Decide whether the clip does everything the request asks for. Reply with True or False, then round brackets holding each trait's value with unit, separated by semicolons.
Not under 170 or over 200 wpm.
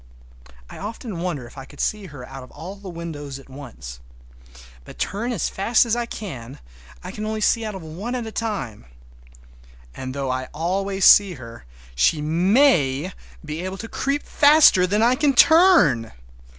True (175 wpm)